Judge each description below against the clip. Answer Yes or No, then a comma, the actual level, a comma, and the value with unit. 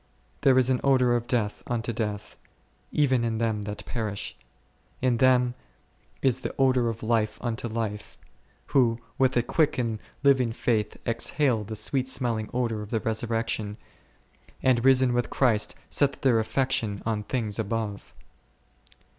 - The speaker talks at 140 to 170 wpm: Yes, average, 145 wpm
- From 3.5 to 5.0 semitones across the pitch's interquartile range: No, average, 2.7 semitones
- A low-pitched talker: Yes, low, 115 Hz